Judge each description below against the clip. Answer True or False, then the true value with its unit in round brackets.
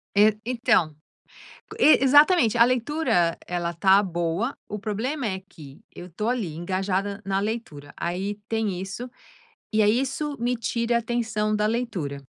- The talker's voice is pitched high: True (210 Hz)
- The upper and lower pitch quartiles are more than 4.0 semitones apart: True (4.7 semitones)